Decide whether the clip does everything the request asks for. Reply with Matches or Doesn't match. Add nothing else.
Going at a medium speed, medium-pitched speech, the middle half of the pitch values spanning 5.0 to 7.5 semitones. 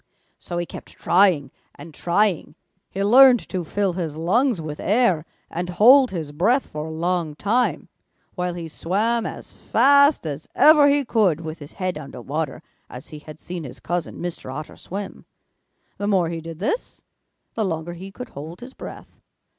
Matches